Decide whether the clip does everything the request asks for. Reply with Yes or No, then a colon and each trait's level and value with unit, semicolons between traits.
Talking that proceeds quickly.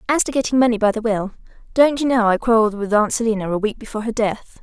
Yes: fast, 260 wpm